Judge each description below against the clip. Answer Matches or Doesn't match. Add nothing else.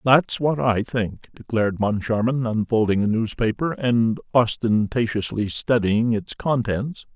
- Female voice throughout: Doesn't match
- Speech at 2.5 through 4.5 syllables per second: Matches